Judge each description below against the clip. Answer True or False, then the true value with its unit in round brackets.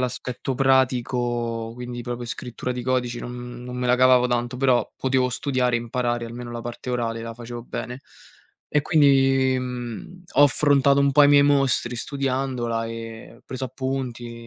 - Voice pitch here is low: True (125 Hz)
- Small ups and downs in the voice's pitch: True (1.8 semitones)